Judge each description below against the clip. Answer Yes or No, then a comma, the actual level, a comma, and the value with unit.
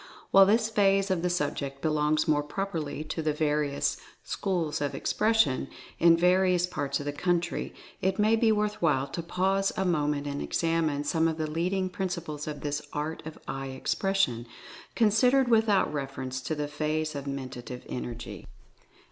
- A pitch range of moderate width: Yes, average, 4.6 semitones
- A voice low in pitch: No, medium, 160 Hz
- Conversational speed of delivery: Yes, average, 170 wpm